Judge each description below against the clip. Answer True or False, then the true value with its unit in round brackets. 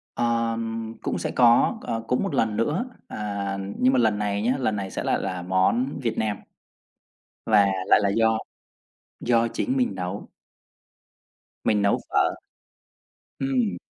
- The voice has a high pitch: False (115 Hz)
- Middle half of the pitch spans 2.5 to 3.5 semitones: True (3.1 semitones)